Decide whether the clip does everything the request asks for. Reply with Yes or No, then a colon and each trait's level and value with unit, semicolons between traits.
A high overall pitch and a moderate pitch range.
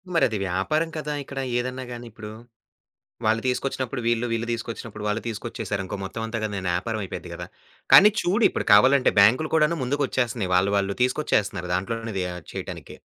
No: low, 115 Hz; average, 4.2 semitones